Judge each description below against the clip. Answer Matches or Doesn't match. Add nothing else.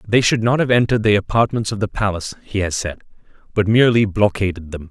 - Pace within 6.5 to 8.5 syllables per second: Matches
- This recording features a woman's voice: Doesn't match